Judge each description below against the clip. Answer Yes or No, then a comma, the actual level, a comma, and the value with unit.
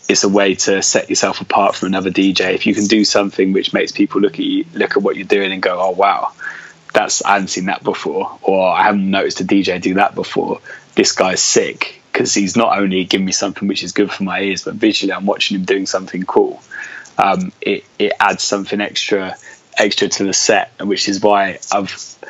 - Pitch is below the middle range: Yes, low, 100 Hz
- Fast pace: Yes, fast, 225 wpm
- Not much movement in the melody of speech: Yes, narrow, 1.4 semitones